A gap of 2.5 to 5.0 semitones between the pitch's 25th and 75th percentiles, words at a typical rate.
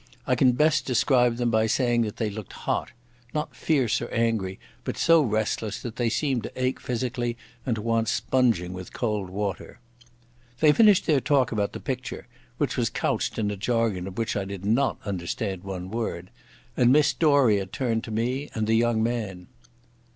Yes: average, 3.4 semitones; average, 175 wpm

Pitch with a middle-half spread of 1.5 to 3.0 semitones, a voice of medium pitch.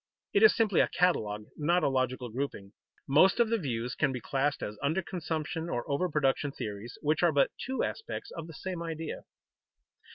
No: average, 5.2 semitones; medium, 150 Hz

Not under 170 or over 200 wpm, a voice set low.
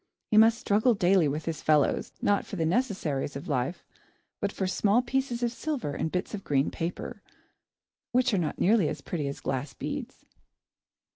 No: average, 175 wpm; medium, 185 Hz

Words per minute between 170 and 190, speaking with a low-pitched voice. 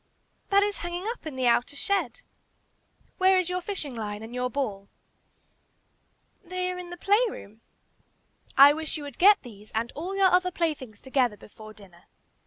No: average, 175 wpm; very high, 300 Hz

